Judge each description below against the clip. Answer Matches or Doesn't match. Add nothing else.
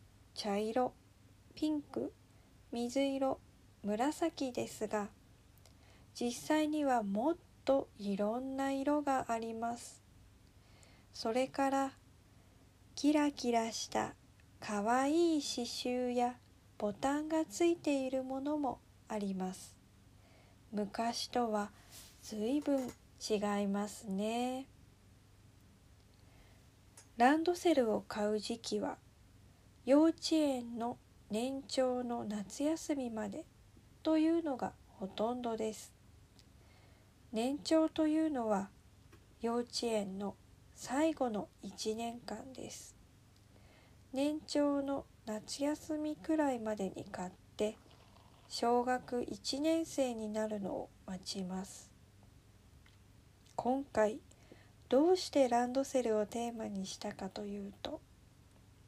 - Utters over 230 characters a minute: Doesn't match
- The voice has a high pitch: Matches